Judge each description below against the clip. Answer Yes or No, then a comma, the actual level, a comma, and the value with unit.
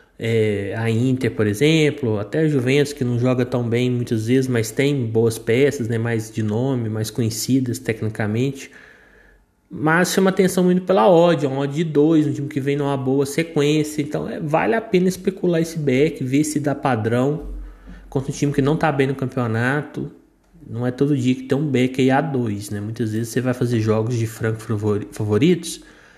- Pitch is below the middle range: Yes, low, 130 Hz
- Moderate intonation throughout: Yes, average, 4.3 semitones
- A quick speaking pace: Yes, fast, 195 wpm